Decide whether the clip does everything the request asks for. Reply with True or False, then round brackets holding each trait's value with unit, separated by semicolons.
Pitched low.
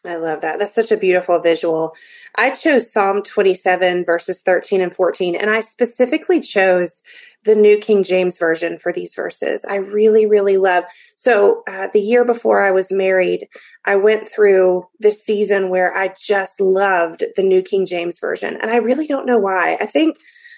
False (195 Hz)